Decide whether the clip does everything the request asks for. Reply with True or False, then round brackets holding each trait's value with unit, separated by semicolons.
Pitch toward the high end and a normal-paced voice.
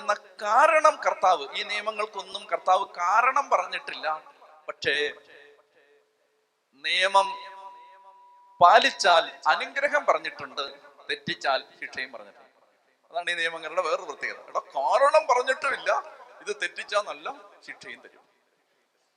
True (255 Hz; 90 wpm)